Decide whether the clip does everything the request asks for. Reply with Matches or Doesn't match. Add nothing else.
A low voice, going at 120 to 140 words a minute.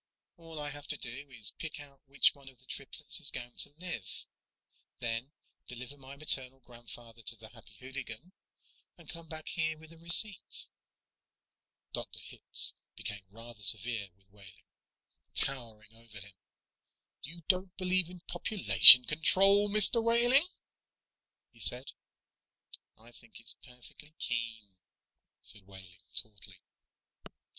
Matches